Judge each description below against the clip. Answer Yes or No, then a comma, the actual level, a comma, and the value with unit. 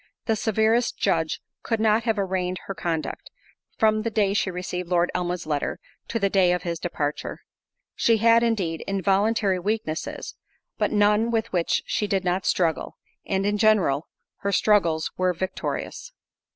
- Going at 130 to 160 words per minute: Yes, average, 155 wpm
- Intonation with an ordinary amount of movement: Yes, average, 3.4 semitones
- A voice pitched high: Yes, high, 195 Hz